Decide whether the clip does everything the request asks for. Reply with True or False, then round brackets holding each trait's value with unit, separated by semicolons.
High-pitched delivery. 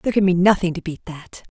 False (180 Hz)